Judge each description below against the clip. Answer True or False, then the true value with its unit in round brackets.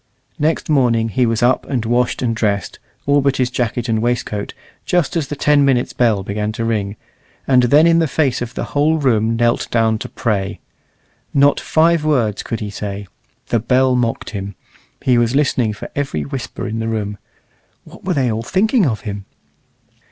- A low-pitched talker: True (120 Hz)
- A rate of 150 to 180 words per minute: False (190 wpm)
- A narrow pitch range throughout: False (4.2 semitones)